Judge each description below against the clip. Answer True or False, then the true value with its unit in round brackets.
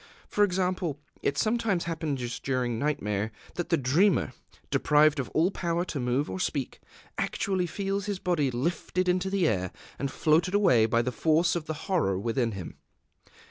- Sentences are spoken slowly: False (165 wpm)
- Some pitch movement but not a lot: False (6.2 semitones)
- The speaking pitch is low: False (155 Hz)